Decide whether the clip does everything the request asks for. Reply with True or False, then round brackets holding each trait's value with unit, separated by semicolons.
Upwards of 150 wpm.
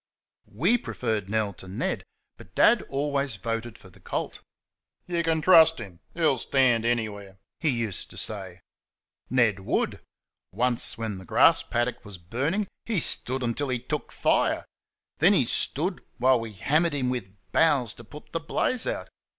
True (160 wpm)